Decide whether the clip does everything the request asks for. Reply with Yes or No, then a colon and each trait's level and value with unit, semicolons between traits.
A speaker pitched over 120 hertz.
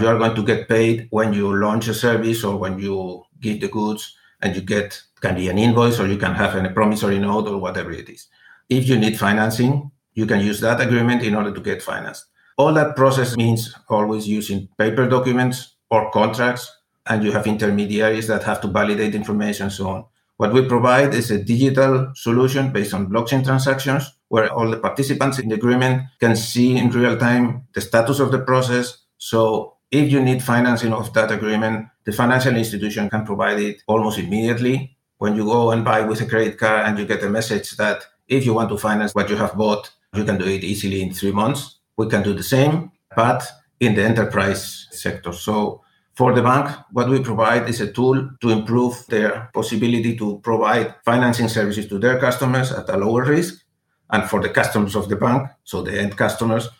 No: low, 115 Hz